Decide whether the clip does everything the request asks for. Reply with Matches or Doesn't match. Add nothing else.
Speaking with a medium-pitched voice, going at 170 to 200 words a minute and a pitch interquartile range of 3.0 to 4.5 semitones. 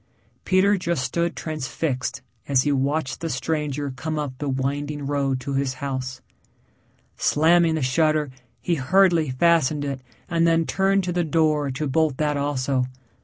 Doesn't match